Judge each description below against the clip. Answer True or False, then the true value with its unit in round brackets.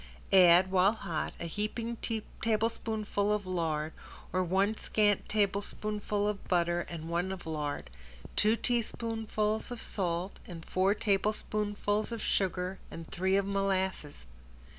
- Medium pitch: False (195 Hz)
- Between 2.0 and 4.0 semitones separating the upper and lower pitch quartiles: True (3.1 semitones)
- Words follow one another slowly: True (125 wpm)